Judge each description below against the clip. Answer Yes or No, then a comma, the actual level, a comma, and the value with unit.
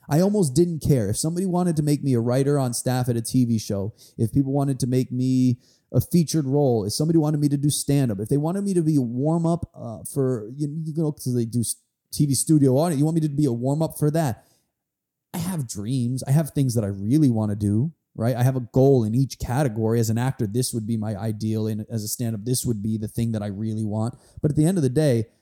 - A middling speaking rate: No, fast, 270 wpm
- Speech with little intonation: No, average, 4.6 semitones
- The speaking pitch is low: Yes, low, 130 Hz